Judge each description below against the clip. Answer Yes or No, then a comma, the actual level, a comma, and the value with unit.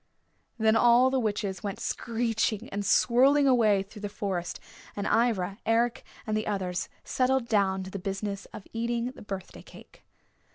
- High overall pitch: Yes, high, 215 Hz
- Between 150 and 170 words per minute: Yes, average, 160 wpm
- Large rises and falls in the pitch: No, average, 3.1 semitones